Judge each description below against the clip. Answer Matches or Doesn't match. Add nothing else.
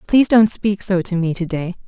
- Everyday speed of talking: Doesn't match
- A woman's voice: Matches